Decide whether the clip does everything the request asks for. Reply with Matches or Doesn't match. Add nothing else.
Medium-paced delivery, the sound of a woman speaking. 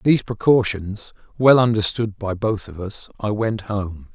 Doesn't match